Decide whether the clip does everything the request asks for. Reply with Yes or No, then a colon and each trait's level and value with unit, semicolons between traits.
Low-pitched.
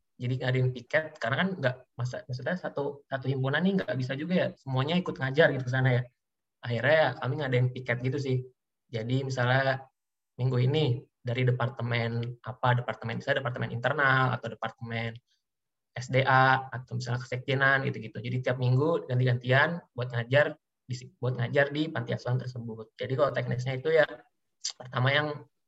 Yes: low, 130 Hz